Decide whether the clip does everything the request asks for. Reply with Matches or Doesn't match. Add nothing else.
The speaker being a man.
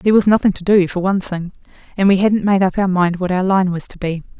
Doesn't match